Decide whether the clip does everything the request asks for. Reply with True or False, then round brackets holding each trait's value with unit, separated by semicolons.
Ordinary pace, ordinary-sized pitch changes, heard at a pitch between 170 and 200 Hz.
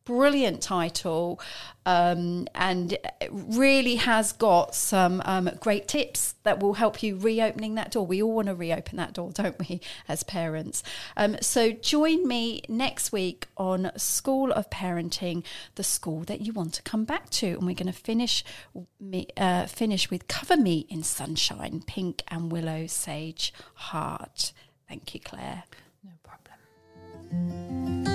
True (150 wpm; 4.7 semitones; 185 Hz)